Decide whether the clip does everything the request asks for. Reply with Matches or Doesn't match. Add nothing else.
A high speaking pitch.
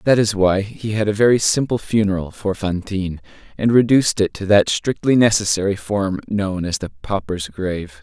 Doesn't match